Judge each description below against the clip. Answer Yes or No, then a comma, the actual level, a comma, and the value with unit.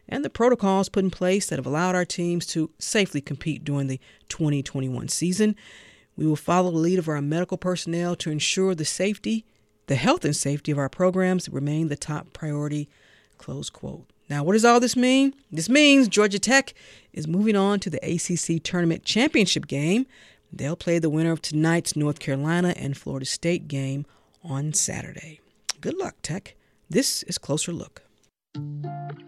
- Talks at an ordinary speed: Yes, average, 170 wpm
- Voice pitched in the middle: Yes, medium, 165 Hz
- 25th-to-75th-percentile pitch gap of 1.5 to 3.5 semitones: No, average, 4.2 semitones